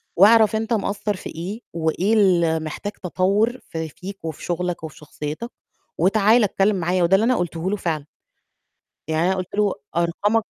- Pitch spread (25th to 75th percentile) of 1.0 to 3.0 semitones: No, average, 3.9 semitones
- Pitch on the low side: No, medium, 185 Hz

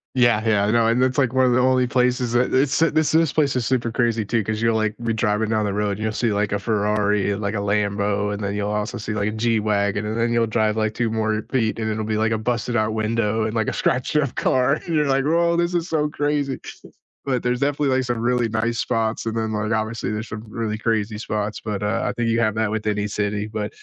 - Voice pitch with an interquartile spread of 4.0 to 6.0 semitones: No, average, 2.7 semitones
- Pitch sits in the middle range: No, low, 110 Hz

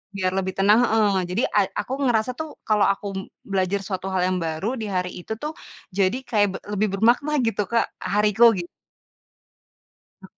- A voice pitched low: No, high, 205 Hz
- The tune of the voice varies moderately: Yes, average, 3.4 semitones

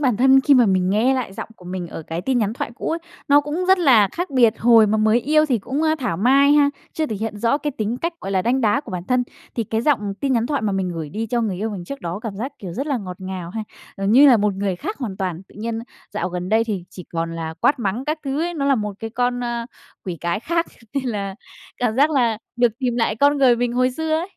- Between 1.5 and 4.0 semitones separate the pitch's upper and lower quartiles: No, wide, 5.4 semitones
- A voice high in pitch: Yes, high, 230 Hz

